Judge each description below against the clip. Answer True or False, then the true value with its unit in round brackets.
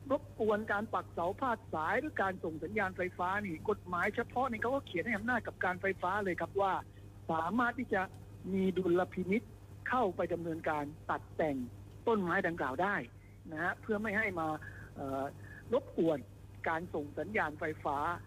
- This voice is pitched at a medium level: True (180 Hz)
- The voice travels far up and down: True (6.2 semitones)